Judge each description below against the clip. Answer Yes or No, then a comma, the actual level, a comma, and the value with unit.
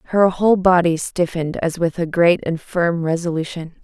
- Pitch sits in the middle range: Yes, medium, 170 Hz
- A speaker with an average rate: Yes, average, 170 wpm